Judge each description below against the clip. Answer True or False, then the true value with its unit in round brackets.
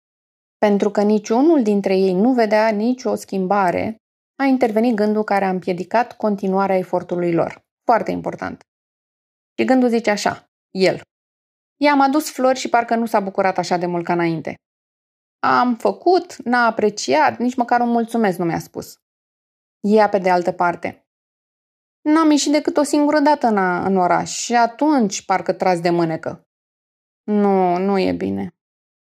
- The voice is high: True (210 Hz)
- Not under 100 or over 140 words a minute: False (150 wpm)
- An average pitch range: True (4.5 semitones)